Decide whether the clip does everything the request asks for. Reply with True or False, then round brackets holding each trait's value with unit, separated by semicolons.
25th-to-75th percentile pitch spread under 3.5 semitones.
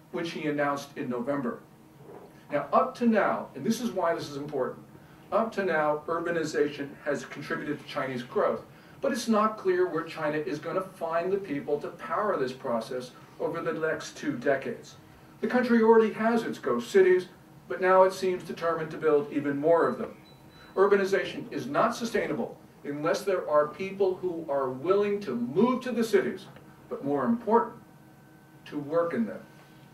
False (4.8 semitones)